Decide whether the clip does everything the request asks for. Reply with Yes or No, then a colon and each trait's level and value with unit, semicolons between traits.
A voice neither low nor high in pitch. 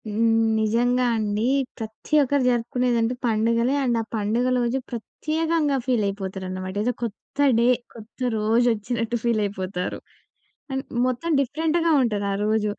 No: high, 230 Hz